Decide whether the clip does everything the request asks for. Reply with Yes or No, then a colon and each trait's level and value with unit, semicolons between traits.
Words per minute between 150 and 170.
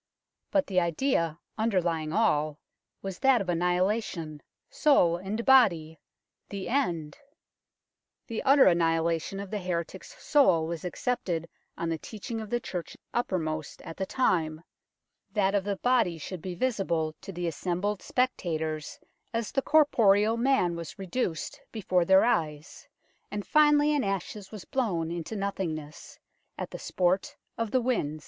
No: average, 140 wpm